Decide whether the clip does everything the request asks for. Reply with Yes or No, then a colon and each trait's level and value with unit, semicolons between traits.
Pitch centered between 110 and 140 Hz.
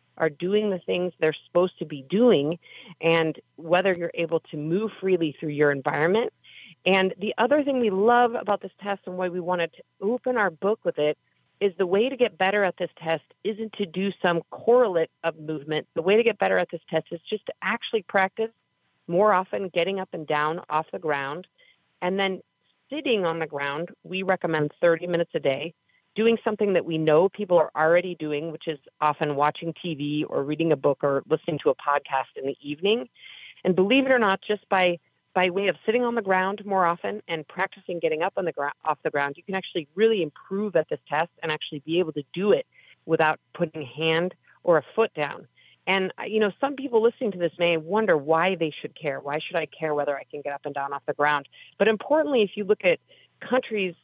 No: medium, 175 Hz